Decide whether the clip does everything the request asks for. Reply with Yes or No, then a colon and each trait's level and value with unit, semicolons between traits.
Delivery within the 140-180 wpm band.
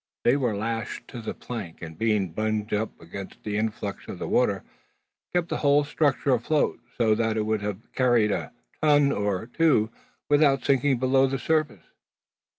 Yes: average, 170 wpm